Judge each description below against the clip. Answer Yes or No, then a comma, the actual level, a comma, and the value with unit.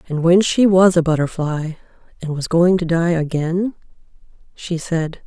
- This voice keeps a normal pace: Yes, average, 160 wpm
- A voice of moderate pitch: Yes, medium, 170 Hz